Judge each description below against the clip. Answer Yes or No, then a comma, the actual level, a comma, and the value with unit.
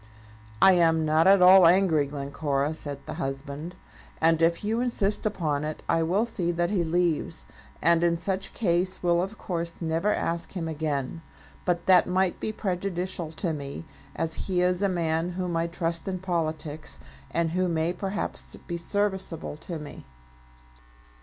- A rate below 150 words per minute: No, average, 165 wpm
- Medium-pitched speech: Yes, medium, 170 Hz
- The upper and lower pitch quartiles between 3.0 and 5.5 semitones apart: No, narrow, 2.6 semitones